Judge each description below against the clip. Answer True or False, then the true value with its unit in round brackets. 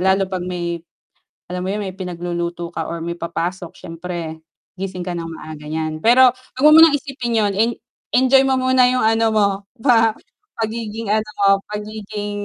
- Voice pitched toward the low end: False (195 Hz)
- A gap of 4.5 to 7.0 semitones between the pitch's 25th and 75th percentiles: True (4.9 semitones)